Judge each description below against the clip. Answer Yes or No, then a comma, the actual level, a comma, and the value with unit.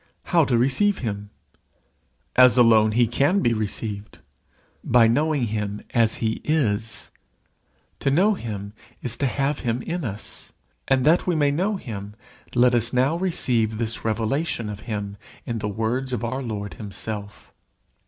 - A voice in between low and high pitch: No, low, 120 Hz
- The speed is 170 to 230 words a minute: No, average, 155 wpm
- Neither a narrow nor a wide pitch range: Yes, average, 4.2 semitones